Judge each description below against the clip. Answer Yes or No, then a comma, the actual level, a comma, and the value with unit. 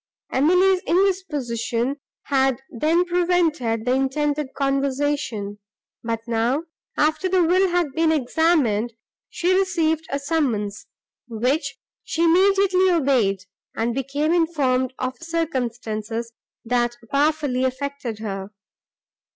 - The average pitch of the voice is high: Yes, very high, 280 Hz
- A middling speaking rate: No, slow, 100 wpm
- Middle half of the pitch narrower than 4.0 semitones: No, wide, 5.5 semitones